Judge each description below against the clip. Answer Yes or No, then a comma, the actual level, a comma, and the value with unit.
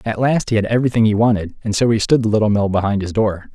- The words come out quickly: Yes, fast, 285 wpm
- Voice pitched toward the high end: No, low, 110 Hz